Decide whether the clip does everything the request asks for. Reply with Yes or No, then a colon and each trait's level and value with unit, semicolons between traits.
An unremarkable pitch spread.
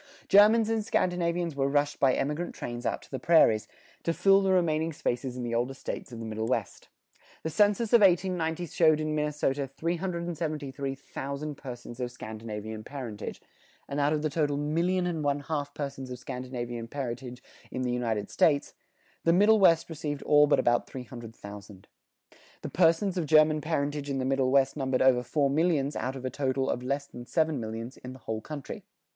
Yes: average, 4.3 semitones